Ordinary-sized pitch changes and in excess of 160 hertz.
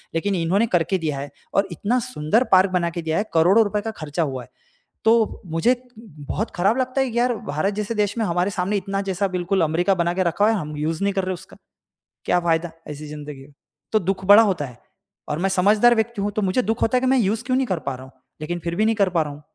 Yes: average, 4.6 semitones; high, 190 Hz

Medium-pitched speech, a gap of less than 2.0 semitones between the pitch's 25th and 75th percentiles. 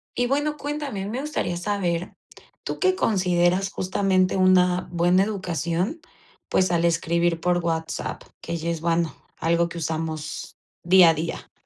No: medium, 175 Hz; narrow, 2.6 semitones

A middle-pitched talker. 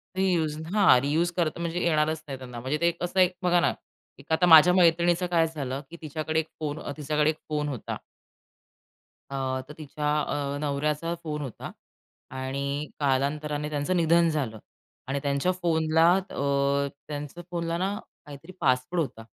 Yes: medium, 155 Hz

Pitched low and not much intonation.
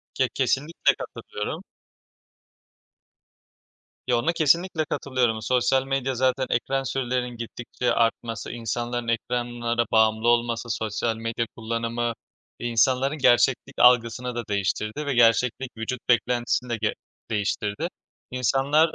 Yes: low, 120 Hz; narrow, 2.1 semitones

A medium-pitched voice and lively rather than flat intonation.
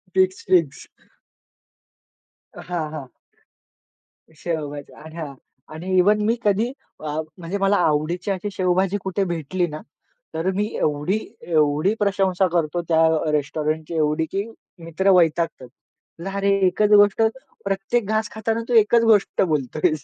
No: medium, 180 Hz; average, 4.2 semitones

